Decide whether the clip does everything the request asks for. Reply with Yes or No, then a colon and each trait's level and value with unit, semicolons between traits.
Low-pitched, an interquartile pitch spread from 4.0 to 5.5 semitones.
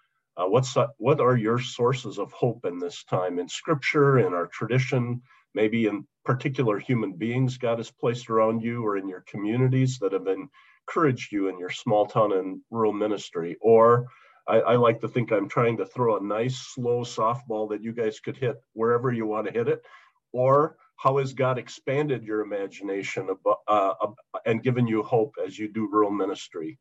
No: low, 115 Hz; average, 3.3 semitones